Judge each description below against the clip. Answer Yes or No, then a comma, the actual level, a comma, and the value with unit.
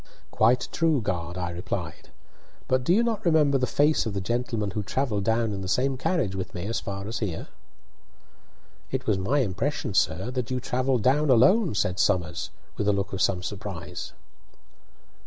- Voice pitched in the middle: No, low, 110 Hz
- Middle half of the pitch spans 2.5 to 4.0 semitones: No, wide, 5.6 semitones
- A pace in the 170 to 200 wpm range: Yes, average, 180 wpm